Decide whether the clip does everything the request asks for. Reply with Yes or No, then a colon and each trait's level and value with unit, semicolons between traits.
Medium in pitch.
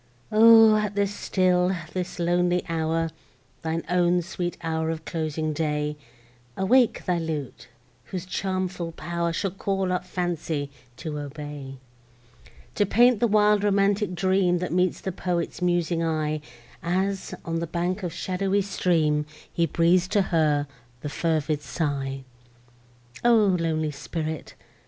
Yes: medium, 175 Hz